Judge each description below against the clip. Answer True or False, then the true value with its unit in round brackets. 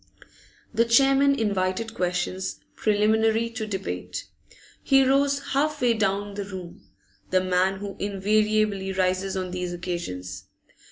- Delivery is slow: True (120 wpm)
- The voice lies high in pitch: True (200 Hz)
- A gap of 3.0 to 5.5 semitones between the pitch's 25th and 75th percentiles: True (3.5 semitones)